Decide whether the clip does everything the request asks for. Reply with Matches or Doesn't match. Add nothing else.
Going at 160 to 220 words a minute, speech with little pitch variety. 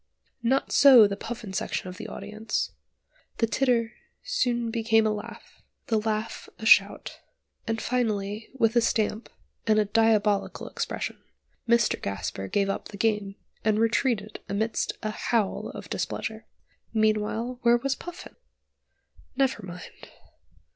Doesn't match